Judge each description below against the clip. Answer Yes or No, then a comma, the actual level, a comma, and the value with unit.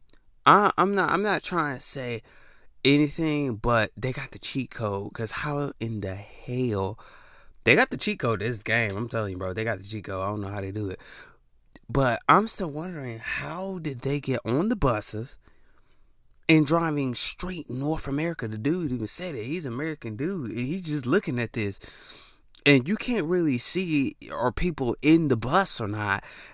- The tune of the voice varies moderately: No, wide, 6.1 semitones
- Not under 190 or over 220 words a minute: Yes, average, 195 wpm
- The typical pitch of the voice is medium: No, low, 130 Hz